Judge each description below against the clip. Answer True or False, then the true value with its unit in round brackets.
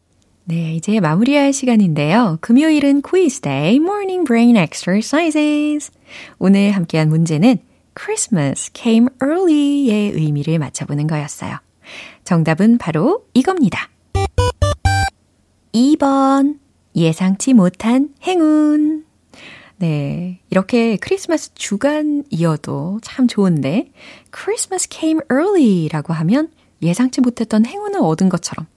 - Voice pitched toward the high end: True (230 Hz)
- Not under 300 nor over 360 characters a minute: True (320 characters per minute)